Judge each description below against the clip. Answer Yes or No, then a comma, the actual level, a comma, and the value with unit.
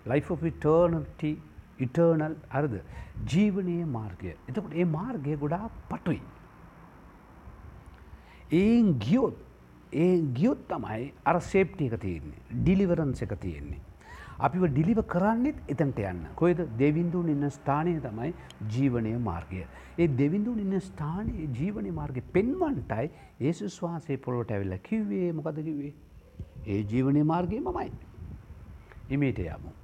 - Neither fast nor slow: No, slow, 95 wpm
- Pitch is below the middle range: No, medium, 145 Hz